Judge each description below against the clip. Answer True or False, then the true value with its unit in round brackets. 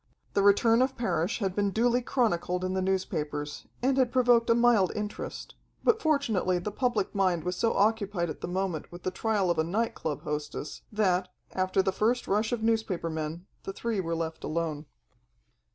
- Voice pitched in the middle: False (195 Hz)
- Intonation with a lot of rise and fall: False (4.7 semitones)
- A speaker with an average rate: True (185 wpm)